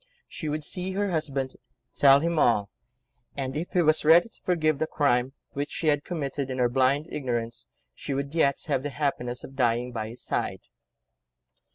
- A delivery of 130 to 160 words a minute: No, average, 185 wpm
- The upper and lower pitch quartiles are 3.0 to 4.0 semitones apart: Yes, average, 3.6 semitones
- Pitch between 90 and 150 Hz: Yes, medium, 140 Hz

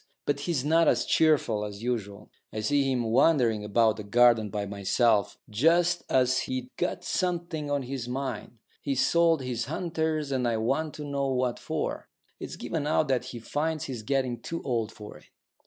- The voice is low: Yes, low, 130 Hz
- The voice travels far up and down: No, average, 5.0 semitones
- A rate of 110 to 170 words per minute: No, average, 185 wpm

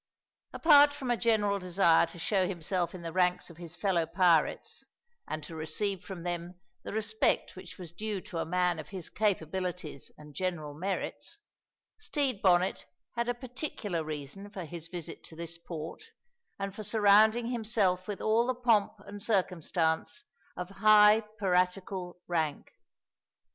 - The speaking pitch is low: No, medium, 185 Hz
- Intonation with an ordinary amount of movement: Yes, average, 3.9 semitones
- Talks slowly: No, average, 155 wpm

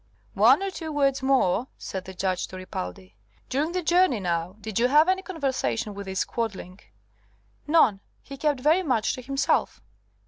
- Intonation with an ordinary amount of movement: No, wide, 8.0 semitones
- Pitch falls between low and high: No, very high, 255 Hz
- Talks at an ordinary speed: Yes, average, 170 wpm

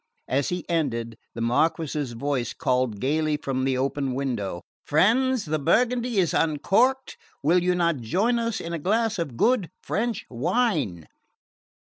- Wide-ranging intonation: Yes, wide, 8.2 semitones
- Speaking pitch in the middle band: Yes, medium, 155 Hz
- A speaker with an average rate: Yes, average, 145 wpm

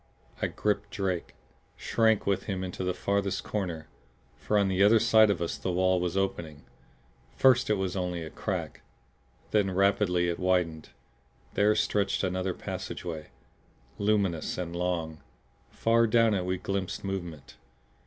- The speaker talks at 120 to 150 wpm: Yes, average, 145 wpm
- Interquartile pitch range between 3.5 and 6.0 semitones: No, narrow, 2.5 semitones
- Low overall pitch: Yes, very low, 95 Hz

